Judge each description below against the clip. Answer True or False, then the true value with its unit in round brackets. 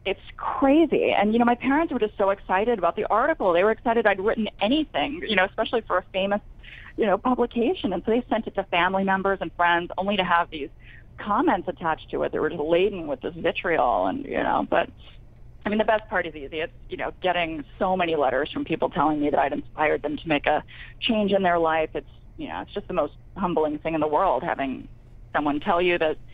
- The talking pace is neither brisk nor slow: False (235 wpm)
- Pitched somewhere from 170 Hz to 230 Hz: True (190 Hz)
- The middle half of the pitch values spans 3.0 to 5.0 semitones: False (5.6 semitones)